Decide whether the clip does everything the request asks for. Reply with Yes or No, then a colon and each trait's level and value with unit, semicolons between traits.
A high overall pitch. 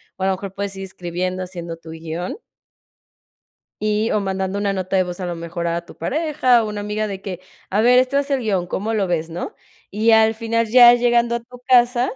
Yes: high, 200 Hz